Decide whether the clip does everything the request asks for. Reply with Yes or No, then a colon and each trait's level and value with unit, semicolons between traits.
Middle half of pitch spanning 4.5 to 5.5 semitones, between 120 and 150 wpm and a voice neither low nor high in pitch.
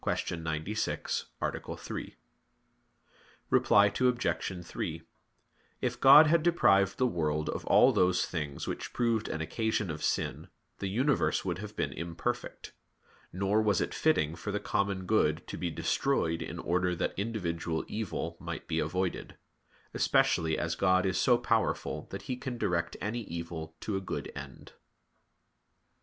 No: average, 4.9 semitones; average, 145 wpm; very low, 95 Hz